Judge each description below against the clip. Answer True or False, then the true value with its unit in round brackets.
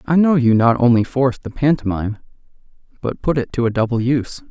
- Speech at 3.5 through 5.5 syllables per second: False (6.2 syllables/s)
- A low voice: True (130 Hz)